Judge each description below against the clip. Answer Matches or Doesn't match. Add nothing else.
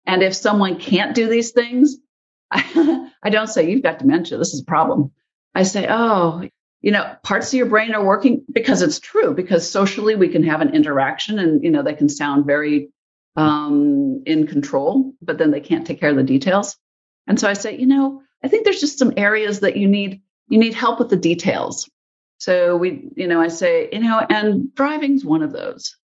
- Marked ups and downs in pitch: Matches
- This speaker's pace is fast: Matches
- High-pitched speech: Matches